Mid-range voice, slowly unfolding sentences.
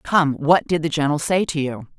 No: medium, 155 Hz; fast, 240 wpm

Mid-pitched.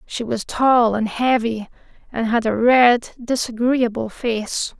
No: high, 235 Hz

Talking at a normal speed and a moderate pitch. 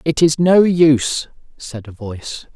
Yes: average, 165 wpm; medium, 145 Hz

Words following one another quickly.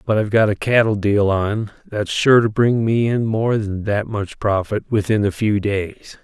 Yes: fast, 210 wpm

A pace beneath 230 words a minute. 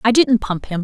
No: fast, 285 wpm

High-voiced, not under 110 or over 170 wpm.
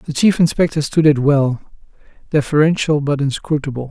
No: medium, 145 Hz; average, 140 wpm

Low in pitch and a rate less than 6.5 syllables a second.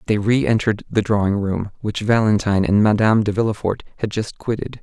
Yes: low, 105 Hz; 6.0 syllables/s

